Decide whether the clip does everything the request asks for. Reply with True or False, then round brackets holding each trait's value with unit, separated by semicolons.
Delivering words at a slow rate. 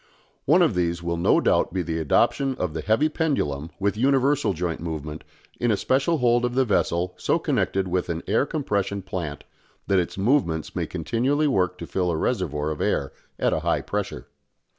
False (190 wpm)